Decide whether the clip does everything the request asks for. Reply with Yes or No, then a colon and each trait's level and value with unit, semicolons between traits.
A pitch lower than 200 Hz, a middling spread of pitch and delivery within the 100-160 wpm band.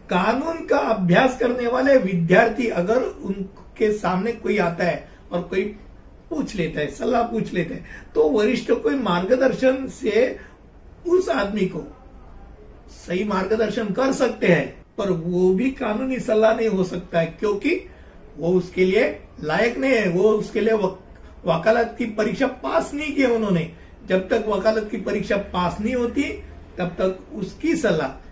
No: high, 215 Hz; average, 4.8 semitones; average, 155 wpm